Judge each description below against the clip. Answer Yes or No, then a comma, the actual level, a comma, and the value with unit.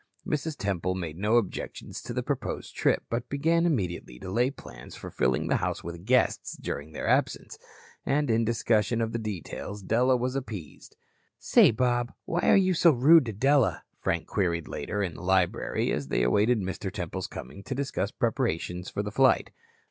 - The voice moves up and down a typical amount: No, wide, 5.8 semitones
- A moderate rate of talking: Yes, average, 180 wpm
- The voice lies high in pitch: No, low, 110 Hz